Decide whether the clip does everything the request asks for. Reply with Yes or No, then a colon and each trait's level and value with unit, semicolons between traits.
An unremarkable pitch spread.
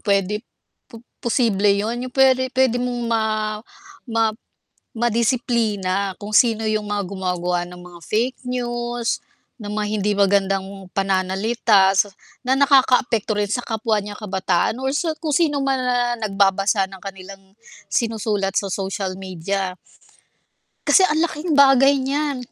Yes: average, 4.2 semitones